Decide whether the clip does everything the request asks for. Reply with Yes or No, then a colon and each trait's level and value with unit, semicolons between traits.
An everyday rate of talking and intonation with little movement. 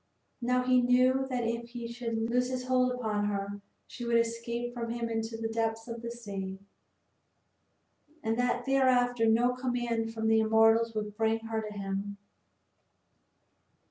Yes: average, 155 wpm; narrow, 1.7 semitones